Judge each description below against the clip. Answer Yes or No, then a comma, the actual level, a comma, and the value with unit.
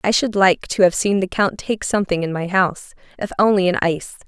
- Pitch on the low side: No, high, 190 Hz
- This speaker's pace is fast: Yes, fast, 240 wpm